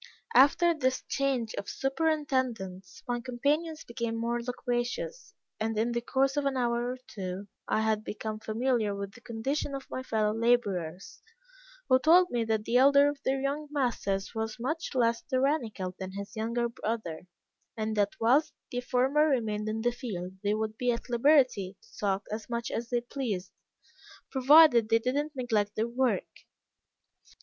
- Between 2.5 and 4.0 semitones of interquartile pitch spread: Yes, average, 3.6 semitones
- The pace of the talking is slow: No, average, 165 wpm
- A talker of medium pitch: No, high, 235 Hz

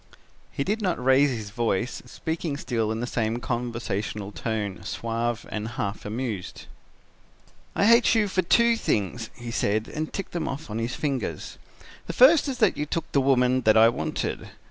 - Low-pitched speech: Yes, low, 120 Hz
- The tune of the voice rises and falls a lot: Yes, wide, 6.0 semitones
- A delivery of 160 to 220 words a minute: Yes, average, 175 wpm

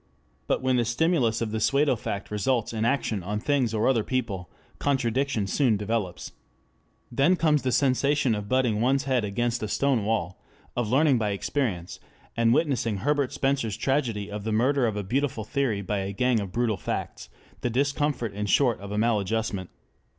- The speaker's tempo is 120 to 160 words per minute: No, average, 180 wpm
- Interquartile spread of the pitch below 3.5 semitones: No, average, 4.4 semitones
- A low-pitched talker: Yes, low, 115 Hz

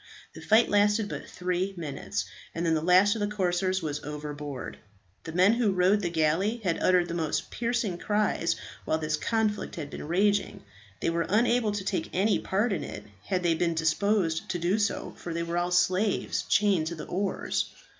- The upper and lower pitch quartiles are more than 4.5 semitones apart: No, average, 3.8 semitones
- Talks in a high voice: No, medium, 180 Hz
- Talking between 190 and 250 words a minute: Yes, average, 195 wpm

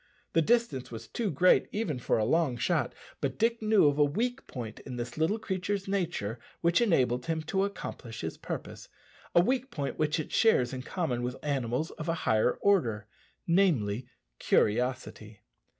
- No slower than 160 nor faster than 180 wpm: Yes, average, 170 wpm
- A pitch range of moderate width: No, wide, 8.1 semitones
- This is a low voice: No, medium, 155 Hz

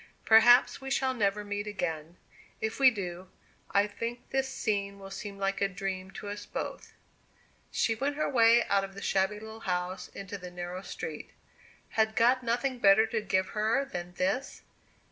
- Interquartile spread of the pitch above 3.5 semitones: No, average, 3.2 semitones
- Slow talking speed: No, average, 175 wpm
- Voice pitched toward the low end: No, high, 205 Hz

